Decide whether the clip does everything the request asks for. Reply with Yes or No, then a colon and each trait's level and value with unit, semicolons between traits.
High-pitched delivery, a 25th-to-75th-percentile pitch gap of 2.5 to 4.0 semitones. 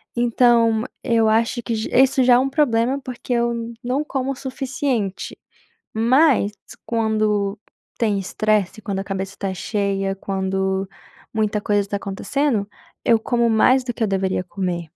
Yes: high, 220 Hz; average, 3.7 semitones